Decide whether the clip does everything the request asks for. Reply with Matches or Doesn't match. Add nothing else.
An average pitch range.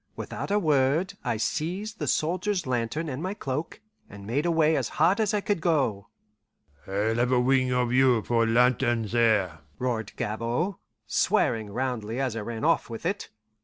Doesn't match